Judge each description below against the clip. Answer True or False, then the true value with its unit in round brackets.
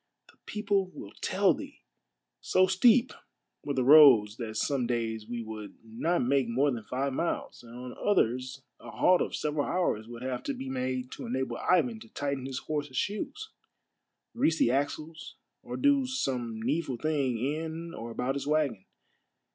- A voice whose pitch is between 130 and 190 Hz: True (135 Hz)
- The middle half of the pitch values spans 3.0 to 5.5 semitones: True (4.9 semitones)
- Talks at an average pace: True (170 wpm)